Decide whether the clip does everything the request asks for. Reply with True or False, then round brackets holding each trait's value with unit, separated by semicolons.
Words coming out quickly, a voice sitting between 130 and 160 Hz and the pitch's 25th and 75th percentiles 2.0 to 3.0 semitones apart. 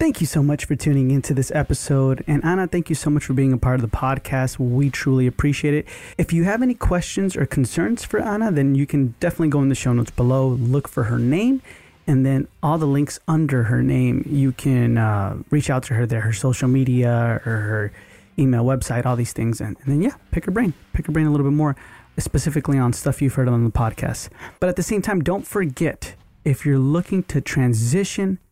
False (230 wpm; 135 Hz; 3.6 semitones)